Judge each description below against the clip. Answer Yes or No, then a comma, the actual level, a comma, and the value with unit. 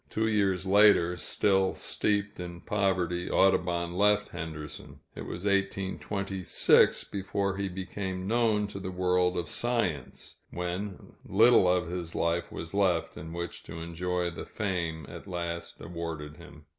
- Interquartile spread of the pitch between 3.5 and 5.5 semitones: No, narrow, 2.5 semitones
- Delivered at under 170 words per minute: Yes, average, 140 wpm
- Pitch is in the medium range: No, very low, 90 Hz